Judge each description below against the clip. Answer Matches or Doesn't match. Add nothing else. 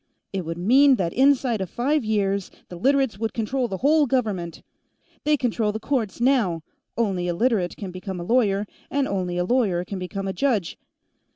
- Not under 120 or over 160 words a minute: Doesn't match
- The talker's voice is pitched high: Matches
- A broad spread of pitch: Matches